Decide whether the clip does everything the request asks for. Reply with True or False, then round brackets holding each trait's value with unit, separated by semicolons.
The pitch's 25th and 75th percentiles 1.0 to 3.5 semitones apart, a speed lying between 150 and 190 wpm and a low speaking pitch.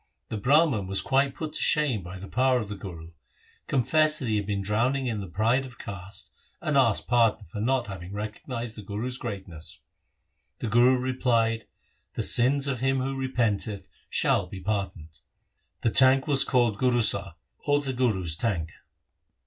False (4.5 semitones; 180 wpm; 115 Hz)